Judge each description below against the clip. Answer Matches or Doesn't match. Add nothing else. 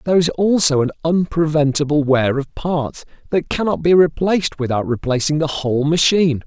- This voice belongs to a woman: Doesn't match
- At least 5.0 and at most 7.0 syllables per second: Matches